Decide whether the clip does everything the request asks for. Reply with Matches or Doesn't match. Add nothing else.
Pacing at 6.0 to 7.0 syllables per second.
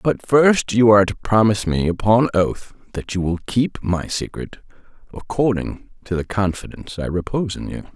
Doesn't match